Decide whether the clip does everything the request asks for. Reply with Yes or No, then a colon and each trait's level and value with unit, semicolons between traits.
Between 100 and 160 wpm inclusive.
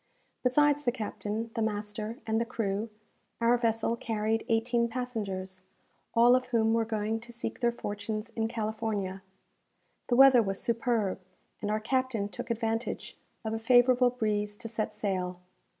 Yes: average, 150 wpm